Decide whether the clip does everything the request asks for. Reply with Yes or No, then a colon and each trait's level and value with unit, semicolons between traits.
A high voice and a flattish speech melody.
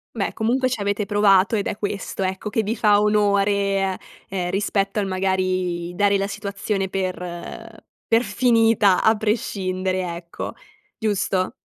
Yes: high, 200 Hz; narrow, 2.0 semitones